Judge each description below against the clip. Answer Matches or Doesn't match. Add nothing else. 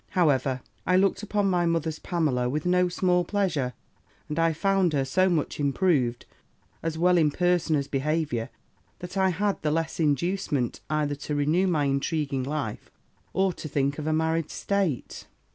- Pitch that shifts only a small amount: Doesn't match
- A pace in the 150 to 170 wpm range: Matches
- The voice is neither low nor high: Matches